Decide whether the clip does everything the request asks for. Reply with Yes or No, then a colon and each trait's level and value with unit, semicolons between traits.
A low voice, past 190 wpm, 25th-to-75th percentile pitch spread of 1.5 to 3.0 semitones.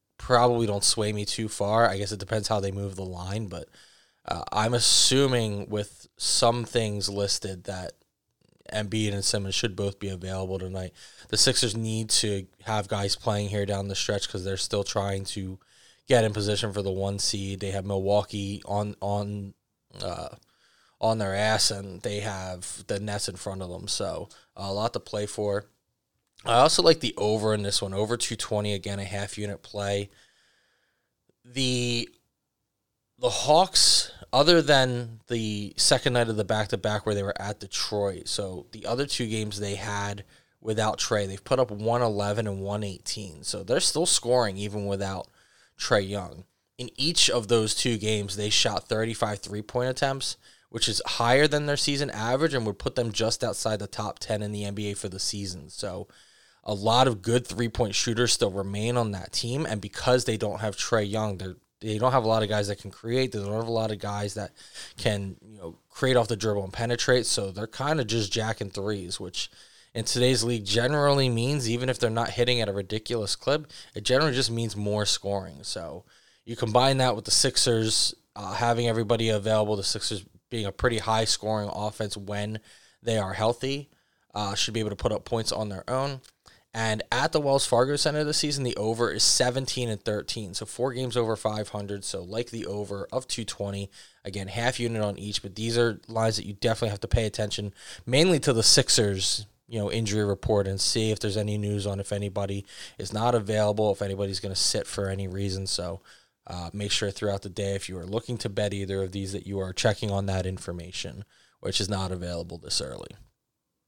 Yes: low, 105 Hz; average, 200 wpm; average, 2.7 semitones